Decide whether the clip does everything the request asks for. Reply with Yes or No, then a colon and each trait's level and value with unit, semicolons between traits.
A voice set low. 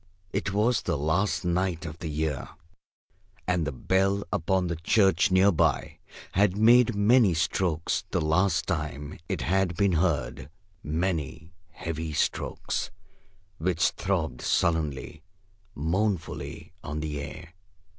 Yes: very low, 85 Hz